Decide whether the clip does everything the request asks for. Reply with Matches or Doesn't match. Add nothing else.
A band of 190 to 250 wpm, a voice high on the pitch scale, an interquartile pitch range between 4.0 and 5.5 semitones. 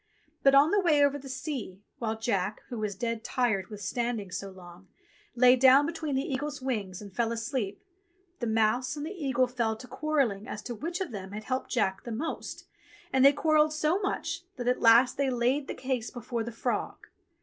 Matches